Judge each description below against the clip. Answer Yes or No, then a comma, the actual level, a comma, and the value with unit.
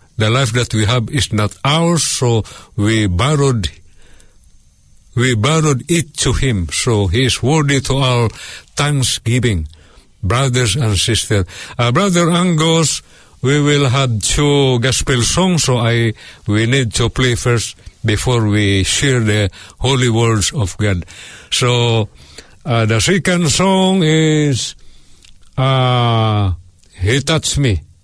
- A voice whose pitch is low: Yes, low, 120 Hz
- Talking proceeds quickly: No, average, 130 wpm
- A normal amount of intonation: Yes, average, 4.9 semitones